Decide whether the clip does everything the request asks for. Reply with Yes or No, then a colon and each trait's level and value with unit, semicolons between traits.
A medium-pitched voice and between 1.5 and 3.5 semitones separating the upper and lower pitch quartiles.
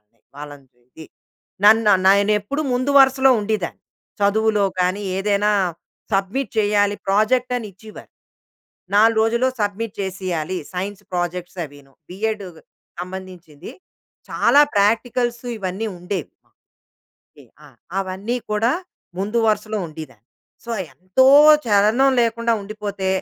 No: high, 205 Hz; average, 3.1 semitones